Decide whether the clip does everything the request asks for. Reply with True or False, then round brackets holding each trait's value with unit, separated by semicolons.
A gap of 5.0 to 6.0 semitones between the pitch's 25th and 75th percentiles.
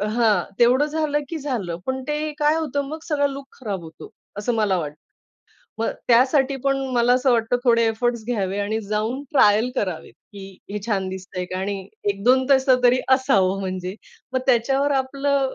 True (5.4 semitones)